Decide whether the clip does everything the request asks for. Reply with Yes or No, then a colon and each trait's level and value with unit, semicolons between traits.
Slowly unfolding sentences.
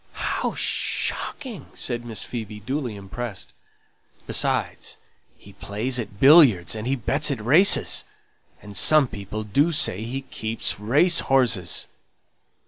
Yes: slow, 125 wpm